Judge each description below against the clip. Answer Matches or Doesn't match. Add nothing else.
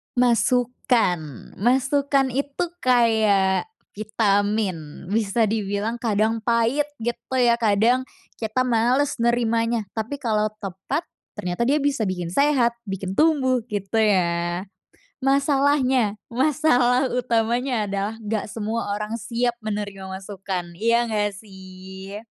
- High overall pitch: Matches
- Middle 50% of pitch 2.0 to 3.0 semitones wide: Doesn't match